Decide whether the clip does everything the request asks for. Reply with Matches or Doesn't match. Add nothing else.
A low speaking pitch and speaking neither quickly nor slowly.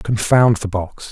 Matches